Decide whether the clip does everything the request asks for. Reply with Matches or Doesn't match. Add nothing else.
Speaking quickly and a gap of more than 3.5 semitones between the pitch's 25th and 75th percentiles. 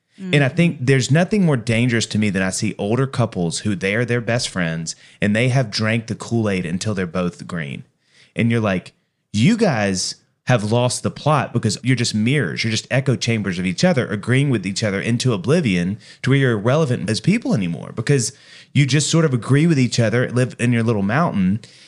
Matches